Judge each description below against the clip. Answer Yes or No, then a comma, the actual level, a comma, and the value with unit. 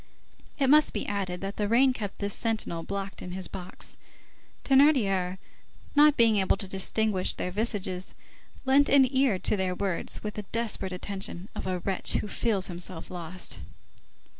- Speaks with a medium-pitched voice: No, high, 200 Hz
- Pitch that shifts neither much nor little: Yes, average, 3.7 semitones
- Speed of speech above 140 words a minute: Yes, average, 165 wpm